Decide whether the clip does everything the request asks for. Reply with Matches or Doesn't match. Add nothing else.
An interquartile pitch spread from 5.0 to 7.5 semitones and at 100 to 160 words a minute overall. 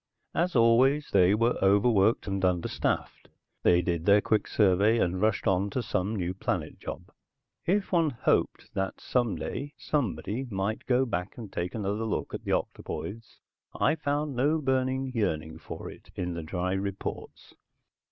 Matches